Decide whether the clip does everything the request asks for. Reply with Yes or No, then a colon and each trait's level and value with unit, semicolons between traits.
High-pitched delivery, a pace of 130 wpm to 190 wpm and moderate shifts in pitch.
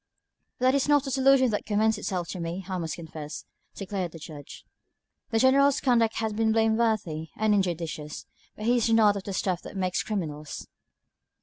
Yes: high, 210 Hz; average, 180 wpm; average, 4.8 semitones